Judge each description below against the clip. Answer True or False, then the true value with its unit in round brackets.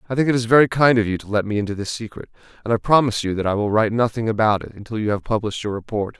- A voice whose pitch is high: False (110 Hz)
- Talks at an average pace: False (300 wpm)